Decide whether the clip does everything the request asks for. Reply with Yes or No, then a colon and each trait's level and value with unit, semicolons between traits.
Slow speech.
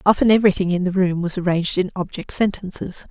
No: average, 195 wpm